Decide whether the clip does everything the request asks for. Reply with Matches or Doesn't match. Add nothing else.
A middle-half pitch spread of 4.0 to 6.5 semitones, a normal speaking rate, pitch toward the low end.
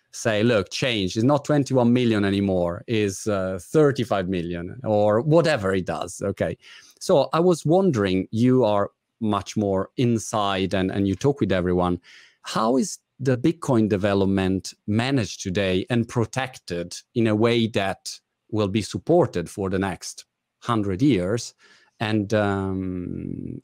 Matches